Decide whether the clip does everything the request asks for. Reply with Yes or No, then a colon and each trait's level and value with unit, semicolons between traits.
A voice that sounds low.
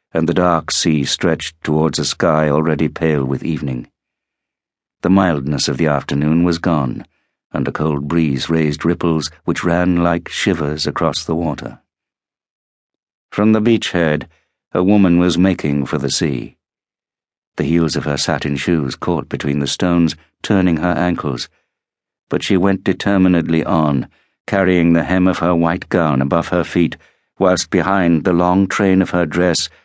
Yes: very low, 85 Hz